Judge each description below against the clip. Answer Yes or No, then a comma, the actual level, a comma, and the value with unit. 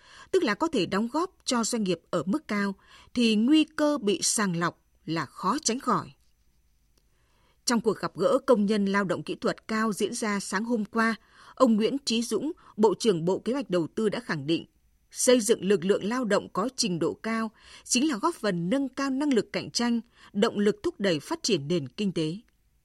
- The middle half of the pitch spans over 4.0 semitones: Yes, average, 4.7 semitones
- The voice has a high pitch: Yes, high, 215 Hz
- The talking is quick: No, average, 215 wpm